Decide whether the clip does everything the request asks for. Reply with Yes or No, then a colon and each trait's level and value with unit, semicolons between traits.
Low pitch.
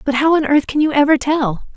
No: very high, 285 Hz